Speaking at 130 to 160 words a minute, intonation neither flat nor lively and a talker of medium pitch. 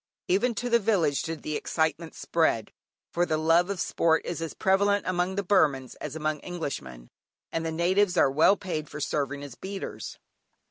No: average, 180 wpm; average, 3.9 semitones; medium, 165 Hz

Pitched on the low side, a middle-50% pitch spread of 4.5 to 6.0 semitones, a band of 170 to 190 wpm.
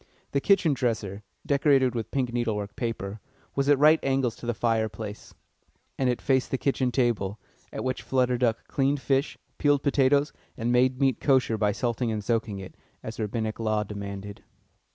No: low, 120 Hz; average, 3.7 semitones; average, 175 wpm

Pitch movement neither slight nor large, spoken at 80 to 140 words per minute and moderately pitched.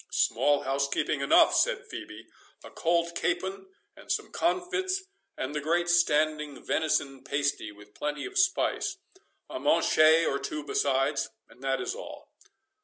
Yes: average, 4.3 semitones; slow, 135 wpm; medium, 150 Hz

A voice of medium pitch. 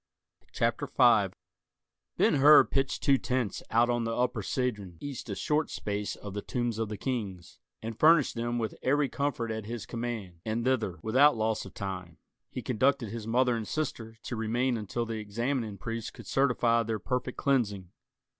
No: low, 115 Hz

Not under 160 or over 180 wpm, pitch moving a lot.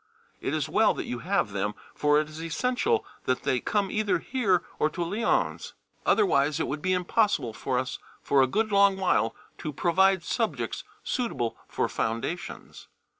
Yes: average, 170 wpm; wide, 7.2 semitones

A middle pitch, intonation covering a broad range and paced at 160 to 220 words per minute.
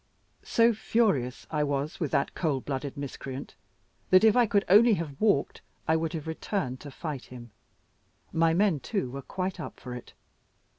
Yes: medium, 160 Hz; wide, 6.2 semitones; average, 170 wpm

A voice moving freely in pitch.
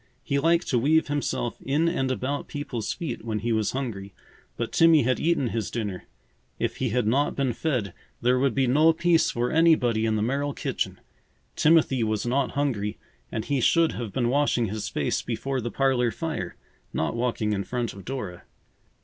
No: average, 4.2 semitones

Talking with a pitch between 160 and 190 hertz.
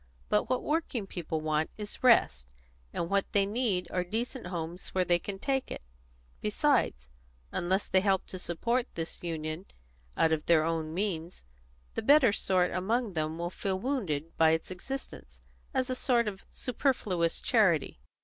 Yes: medium, 185 Hz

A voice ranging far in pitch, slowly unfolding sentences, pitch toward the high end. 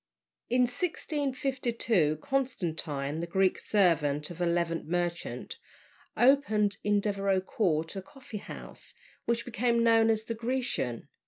Yes: wide, 6.0 semitones; slow, 120 wpm; high, 205 Hz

